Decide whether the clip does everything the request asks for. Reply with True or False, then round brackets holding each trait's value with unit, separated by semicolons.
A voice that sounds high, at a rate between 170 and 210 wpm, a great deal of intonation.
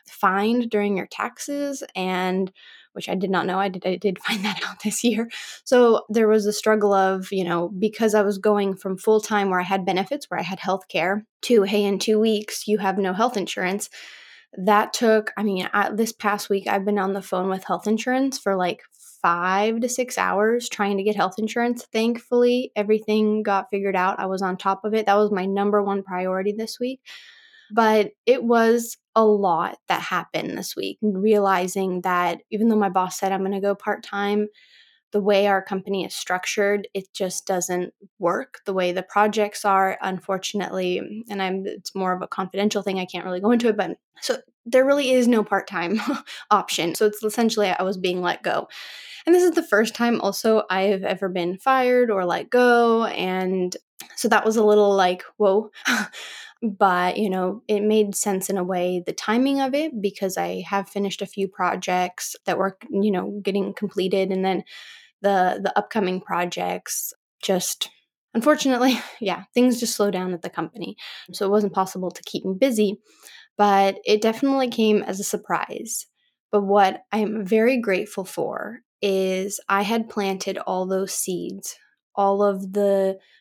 False (205 Hz; 190 wpm; 2.6 semitones)